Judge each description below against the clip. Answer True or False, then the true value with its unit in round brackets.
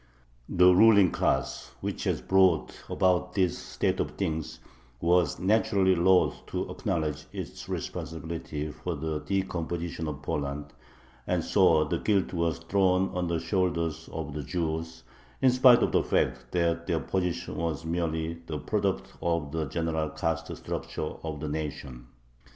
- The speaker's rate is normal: True (145 wpm)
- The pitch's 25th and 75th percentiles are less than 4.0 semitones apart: True (2.7 semitones)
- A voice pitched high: False (85 Hz)